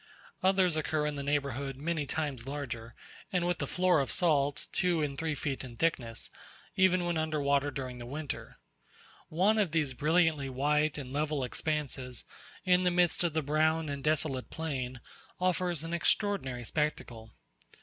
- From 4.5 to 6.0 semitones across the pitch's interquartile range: No, average, 3.4 semitones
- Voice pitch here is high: No, medium, 150 Hz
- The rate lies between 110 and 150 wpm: No, average, 160 wpm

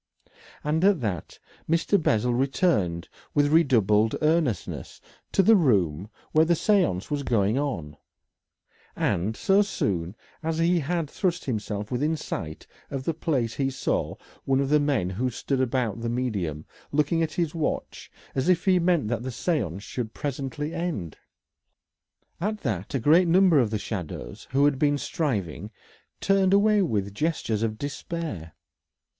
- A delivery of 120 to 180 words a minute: Yes, average, 150 wpm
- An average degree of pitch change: No, wide, 7.5 semitones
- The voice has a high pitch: No, low, 135 Hz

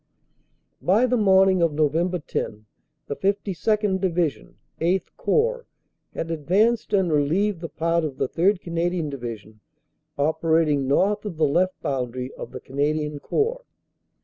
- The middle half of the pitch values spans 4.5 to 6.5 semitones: Yes, average, 4.8 semitones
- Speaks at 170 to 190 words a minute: No, average, 145 wpm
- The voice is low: No, medium, 170 Hz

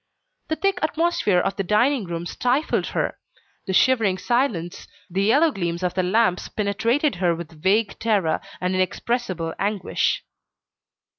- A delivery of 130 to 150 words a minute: Yes, average, 140 wpm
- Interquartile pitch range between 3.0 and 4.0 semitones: No, average, 5.3 semitones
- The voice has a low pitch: No, high, 200 Hz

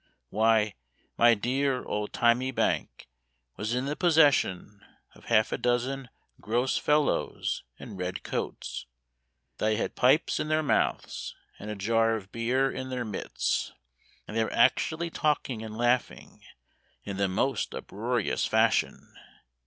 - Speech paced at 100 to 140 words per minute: Yes, slow, 135 wpm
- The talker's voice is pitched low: Yes, low, 120 Hz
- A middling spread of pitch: Yes, average, 3.6 semitones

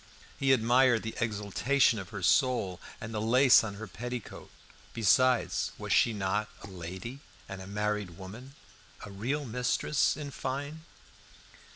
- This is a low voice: Yes, low, 115 Hz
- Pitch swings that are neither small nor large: Yes, average, 4.2 semitones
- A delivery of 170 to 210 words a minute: No, average, 145 wpm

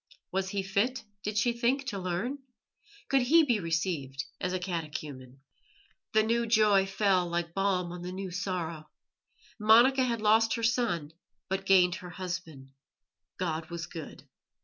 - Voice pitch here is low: No, high, 190 Hz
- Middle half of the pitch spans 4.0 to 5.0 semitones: Yes, average, 4.4 semitones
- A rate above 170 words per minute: No, average, 150 wpm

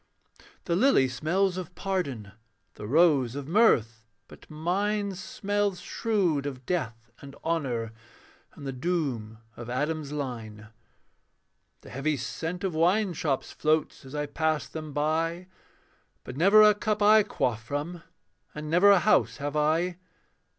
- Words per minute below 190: Yes, average, 140 wpm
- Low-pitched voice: No, medium, 155 Hz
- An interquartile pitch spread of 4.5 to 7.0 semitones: Yes, average, 5.3 semitones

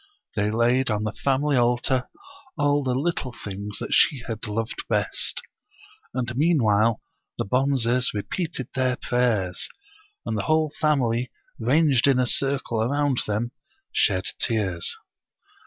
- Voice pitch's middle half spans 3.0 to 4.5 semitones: Yes, average, 3.8 semitones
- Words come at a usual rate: No, slow, 130 wpm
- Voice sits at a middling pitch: No, low, 125 Hz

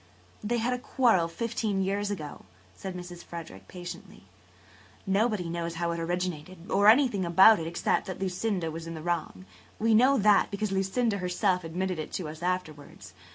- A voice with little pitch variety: No, average, 3.6 semitones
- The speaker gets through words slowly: No, average, 175 wpm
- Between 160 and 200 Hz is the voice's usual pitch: Yes, medium, 185 Hz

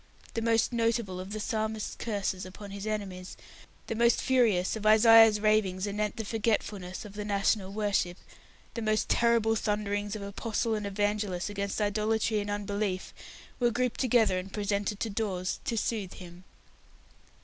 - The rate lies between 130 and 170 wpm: Yes, average, 155 wpm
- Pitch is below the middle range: No, high, 210 Hz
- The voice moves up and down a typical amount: No, narrow, 1.9 semitones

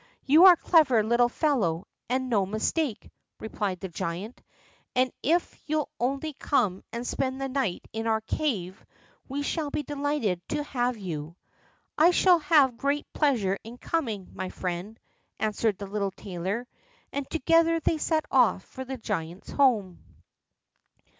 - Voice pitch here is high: Yes, high, 245 Hz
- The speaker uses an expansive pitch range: Yes, wide, 6.5 semitones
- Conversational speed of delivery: Yes, average, 150 wpm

